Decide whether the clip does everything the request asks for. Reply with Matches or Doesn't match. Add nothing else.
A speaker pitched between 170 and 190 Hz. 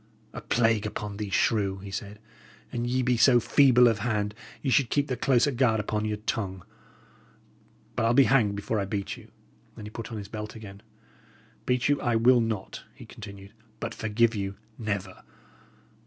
Doesn't match